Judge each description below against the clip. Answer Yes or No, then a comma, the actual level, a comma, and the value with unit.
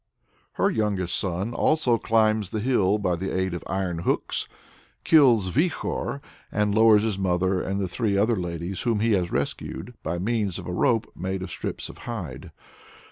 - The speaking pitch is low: Yes, low, 100 Hz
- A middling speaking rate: Yes, average, 165 wpm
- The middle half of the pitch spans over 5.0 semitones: No, average, 3.6 semitones